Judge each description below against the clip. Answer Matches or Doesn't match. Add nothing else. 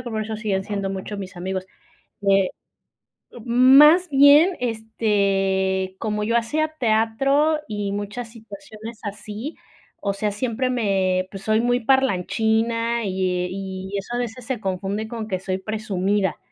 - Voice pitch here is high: Matches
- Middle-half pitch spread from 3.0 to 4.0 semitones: Matches